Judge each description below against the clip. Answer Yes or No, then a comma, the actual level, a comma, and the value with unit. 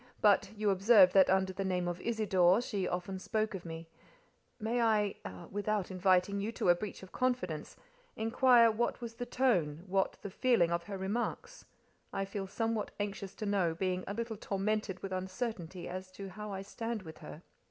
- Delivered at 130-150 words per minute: No, average, 175 wpm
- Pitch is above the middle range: Yes, high, 195 Hz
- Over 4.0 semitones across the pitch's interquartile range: No, average, 3.2 semitones